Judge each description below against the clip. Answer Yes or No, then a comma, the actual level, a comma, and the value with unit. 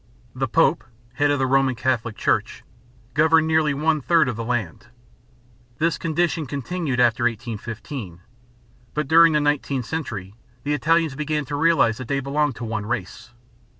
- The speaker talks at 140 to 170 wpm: Yes, average, 155 wpm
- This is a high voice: No, medium, 140 Hz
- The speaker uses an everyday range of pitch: Yes, average, 4.3 semitones